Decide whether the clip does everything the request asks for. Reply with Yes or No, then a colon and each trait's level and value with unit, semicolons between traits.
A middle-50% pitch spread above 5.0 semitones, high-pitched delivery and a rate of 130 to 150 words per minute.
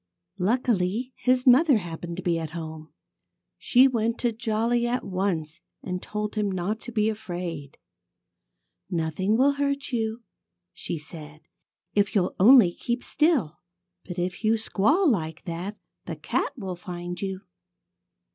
Yes: wide, 5.5 semitones; high, 200 Hz; average, 140 wpm